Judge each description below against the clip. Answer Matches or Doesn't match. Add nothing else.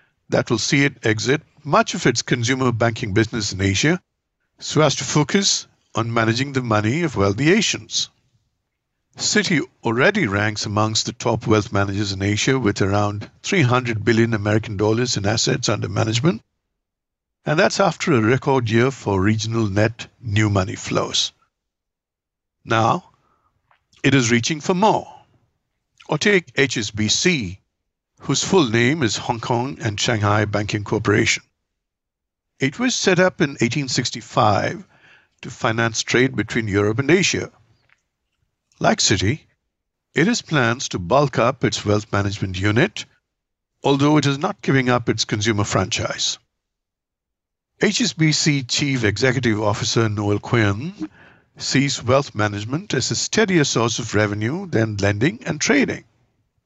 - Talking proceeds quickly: Doesn't match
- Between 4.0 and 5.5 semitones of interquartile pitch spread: Matches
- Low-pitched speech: Matches